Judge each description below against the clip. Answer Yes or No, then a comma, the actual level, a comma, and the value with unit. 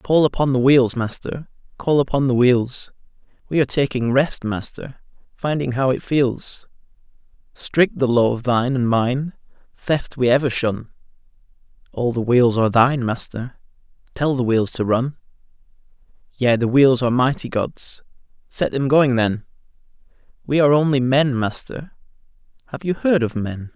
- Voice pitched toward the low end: Yes, low, 130 Hz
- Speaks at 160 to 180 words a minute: No, average, 145 wpm